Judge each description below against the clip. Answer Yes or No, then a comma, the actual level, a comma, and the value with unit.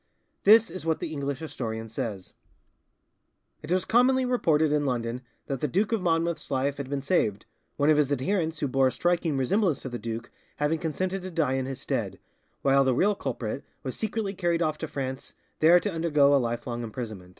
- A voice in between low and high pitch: Yes, medium, 145 Hz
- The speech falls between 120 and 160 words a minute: No, average, 195 wpm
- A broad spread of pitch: No, average, 5.0 semitones